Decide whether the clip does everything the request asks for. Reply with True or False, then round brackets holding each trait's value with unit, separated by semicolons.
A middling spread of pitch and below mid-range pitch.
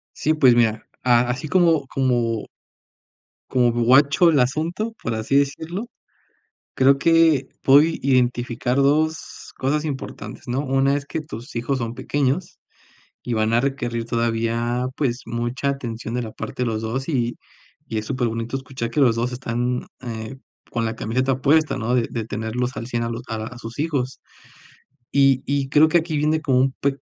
True (3.2 semitones; 130 Hz)